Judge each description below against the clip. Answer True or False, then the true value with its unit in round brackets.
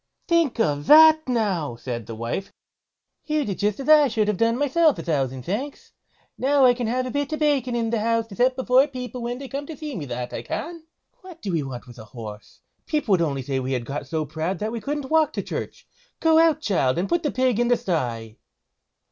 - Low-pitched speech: False (230 Hz)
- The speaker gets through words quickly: True (240 wpm)